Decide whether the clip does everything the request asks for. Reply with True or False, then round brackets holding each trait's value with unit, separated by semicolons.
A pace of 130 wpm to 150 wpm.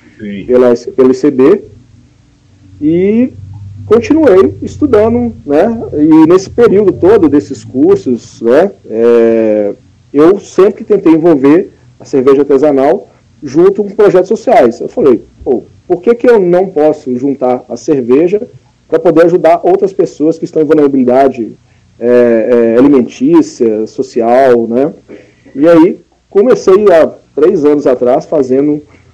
False (120 wpm)